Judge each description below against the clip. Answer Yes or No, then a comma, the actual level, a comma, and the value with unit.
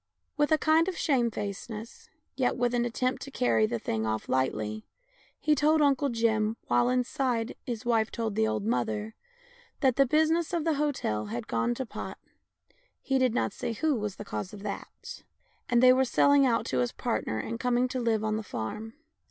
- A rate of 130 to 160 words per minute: No, average, 195 wpm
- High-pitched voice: Yes, high, 235 Hz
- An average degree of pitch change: No, wide, 6.6 semitones